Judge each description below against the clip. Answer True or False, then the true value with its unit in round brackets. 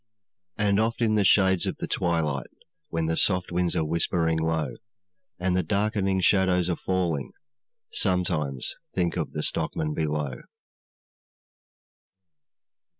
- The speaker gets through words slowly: True (125 wpm)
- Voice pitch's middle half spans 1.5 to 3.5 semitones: True (2.9 semitones)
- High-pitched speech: False (90 Hz)